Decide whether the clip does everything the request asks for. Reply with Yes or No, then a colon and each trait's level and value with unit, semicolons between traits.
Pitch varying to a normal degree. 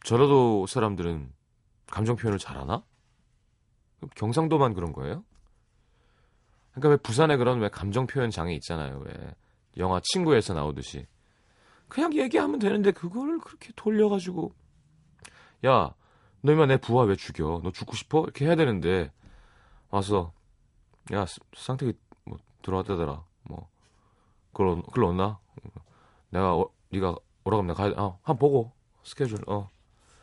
No: wide, 7.1 semitones